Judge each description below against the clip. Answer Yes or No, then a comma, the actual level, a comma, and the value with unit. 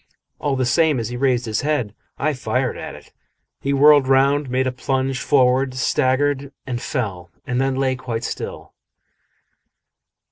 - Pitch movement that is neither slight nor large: No, narrow, 1.8 semitones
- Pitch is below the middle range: Yes, low, 130 Hz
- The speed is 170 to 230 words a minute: No, average, 155 wpm